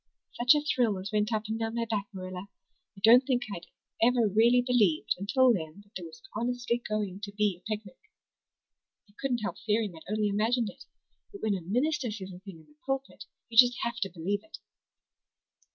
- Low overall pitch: No, high, 215 Hz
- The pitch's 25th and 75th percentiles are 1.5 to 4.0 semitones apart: Yes, average, 3.7 semitones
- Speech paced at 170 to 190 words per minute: No, average, 200 wpm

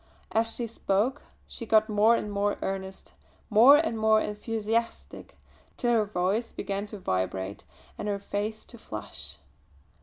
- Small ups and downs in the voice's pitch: Yes, narrow, 2.2 semitones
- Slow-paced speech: No, average, 145 wpm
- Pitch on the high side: Yes, high, 210 Hz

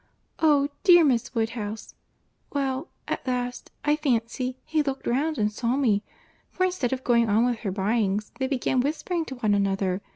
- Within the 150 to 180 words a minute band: Yes, average, 165 wpm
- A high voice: Yes, very high, 250 Hz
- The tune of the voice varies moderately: Yes, average, 4.4 semitones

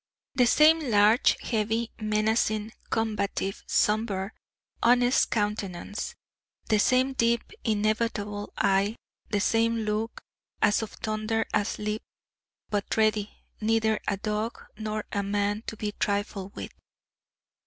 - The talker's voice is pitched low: No, high, 215 Hz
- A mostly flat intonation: Yes, narrow, 1.5 semitones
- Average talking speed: No, slow, 110 wpm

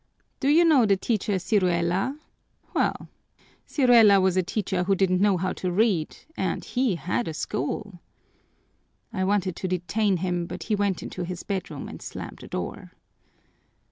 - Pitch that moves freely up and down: No, average, 2.9 semitones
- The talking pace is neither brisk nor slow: Yes, average, 160 wpm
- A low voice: No, high, 190 Hz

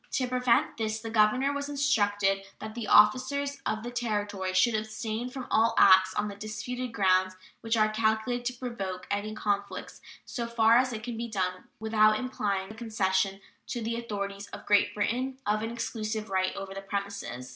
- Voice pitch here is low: No, high, 215 Hz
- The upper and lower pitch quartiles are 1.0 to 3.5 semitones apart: Yes, average, 2.9 semitones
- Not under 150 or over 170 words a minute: No, average, 180 wpm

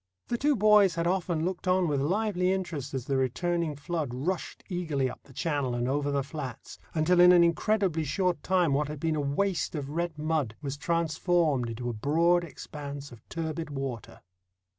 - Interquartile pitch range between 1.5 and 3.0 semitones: No, average, 4.0 semitones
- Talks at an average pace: Yes, average, 185 wpm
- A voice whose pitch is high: No, medium, 155 Hz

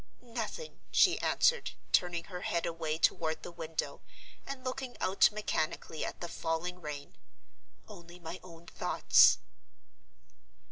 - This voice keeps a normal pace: No, slow, 125 wpm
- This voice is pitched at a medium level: Yes, medium, 175 Hz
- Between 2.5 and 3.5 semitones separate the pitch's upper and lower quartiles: No, average, 4.3 semitones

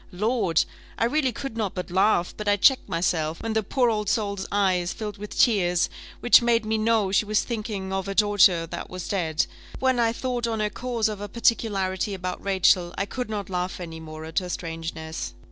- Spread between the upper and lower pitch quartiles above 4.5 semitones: No, average, 3.8 semitones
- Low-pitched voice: No, high, 200 Hz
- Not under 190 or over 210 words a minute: Yes, fast, 205 wpm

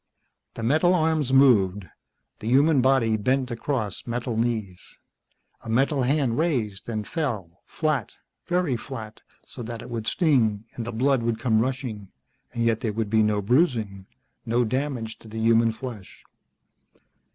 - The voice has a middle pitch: No, low, 115 Hz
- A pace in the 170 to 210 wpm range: No, average, 150 wpm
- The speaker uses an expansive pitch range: No, average, 3.4 semitones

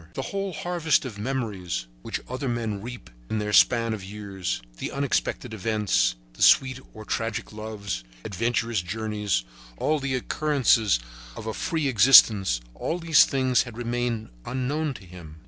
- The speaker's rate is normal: Yes, average, 145 wpm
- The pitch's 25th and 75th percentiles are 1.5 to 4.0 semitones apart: No, average, 4.4 semitones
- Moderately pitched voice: No, low, 115 Hz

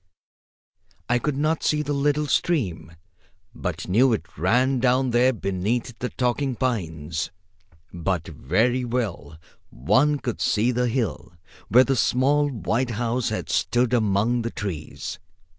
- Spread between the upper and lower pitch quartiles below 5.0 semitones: No, average, 5.3 semitones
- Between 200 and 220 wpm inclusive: No, slow, 135 wpm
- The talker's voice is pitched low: Yes, low, 120 Hz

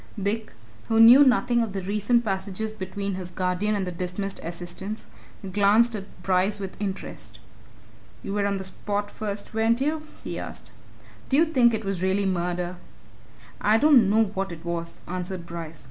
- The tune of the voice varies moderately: Yes, average, 3.1 semitones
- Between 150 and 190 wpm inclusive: Yes, average, 170 wpm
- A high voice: Yes, high, 200 Hz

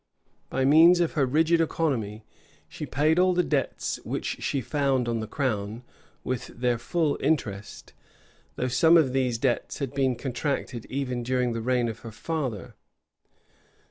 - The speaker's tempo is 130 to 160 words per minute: Yes, average, 155 wpm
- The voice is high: No, low, 130 Hz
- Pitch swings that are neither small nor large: Yes, average, 4.2 semitones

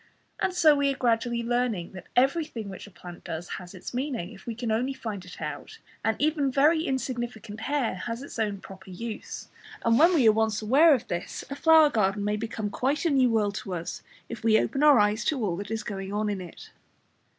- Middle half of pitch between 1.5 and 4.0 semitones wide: No, average, 4.8 semitones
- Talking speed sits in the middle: No, fast, 225 wpm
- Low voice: No, high, 225 Hz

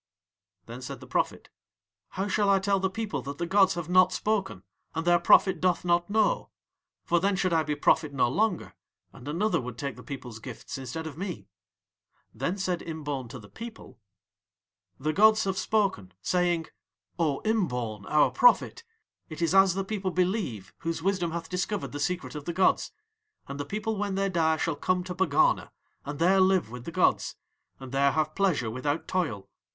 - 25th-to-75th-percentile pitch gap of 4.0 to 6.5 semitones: Yes, average, 5.1 semitones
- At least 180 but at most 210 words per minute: Yes, average, 185 wpm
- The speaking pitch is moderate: Yes, medium, 175 Hz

